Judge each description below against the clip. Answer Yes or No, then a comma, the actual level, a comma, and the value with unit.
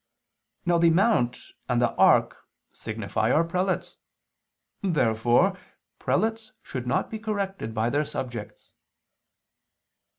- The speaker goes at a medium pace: No, slow, 105 wpm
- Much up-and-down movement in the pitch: Yes, wide, 8.2 semitones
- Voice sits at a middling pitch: Yes, medium, 165 Hz